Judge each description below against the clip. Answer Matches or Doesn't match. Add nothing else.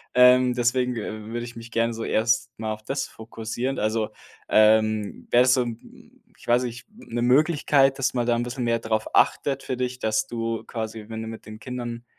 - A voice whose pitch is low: Matches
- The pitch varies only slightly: Matches